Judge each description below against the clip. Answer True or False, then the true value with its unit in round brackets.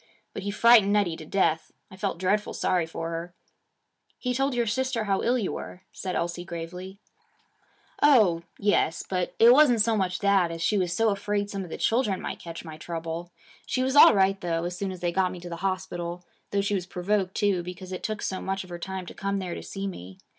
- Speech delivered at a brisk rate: True (225 wpm)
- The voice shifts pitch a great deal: False (2.9 semitones)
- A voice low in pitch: False (190 Hz)